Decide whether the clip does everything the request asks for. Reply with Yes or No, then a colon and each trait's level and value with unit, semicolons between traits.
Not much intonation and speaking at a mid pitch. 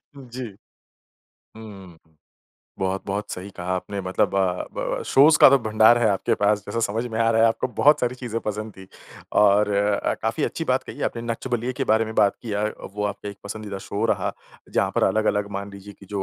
No: narrow, 2.3 semitones; low, 105 Hz